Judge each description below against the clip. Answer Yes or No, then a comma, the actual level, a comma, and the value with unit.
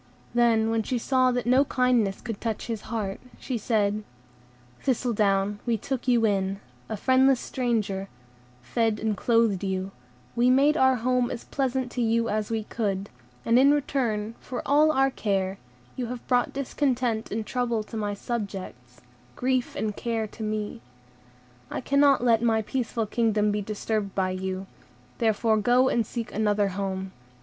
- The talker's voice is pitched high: Yes, high, 225 Hz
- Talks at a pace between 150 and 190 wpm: Yes, average, 160 wpm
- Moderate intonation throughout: Yes, average, 3.2 semitones